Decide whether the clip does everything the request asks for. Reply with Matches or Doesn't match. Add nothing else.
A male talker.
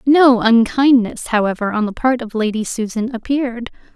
Doesn't match